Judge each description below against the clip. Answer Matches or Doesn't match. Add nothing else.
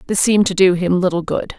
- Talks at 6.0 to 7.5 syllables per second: Matches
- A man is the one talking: Doesn't match